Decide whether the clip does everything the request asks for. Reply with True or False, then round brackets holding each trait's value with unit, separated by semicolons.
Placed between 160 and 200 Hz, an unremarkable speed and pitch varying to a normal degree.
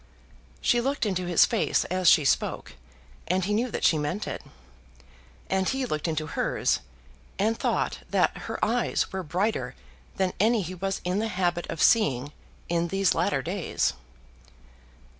True (185 Hz; 160 wpm; 3.7 semitones)